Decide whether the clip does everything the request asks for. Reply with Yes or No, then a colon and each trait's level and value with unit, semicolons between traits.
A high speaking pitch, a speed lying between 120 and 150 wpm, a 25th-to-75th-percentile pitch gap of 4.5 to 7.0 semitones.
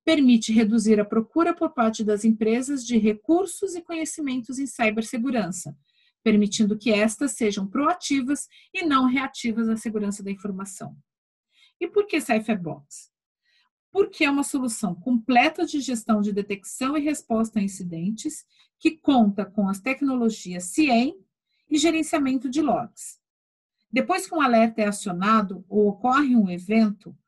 Yes: high, 230 Hz; average, 140 wpm; wide, 5.6 semitones